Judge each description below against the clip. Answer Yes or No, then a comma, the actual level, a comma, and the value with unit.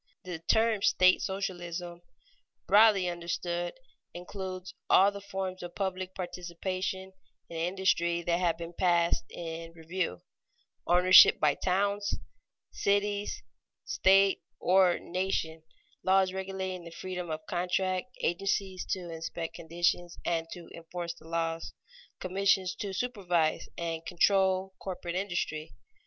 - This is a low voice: No, medium, 180 Hz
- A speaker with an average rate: No, slow, 115 wpm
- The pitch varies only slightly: Yes, narrow, 2.0 semitones